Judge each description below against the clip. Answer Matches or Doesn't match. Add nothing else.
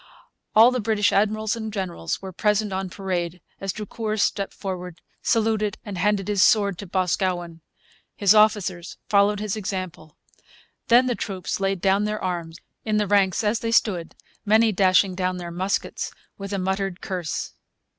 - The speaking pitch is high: Matches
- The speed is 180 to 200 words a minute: Doesn't match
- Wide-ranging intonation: Doesn't match